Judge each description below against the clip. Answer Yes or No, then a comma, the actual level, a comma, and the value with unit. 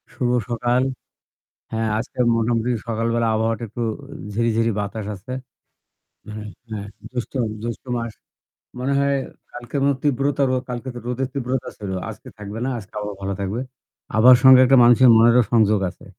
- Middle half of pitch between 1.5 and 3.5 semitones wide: Yes, narrow, 2.4 semitones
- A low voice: Yes, low, 115 Hz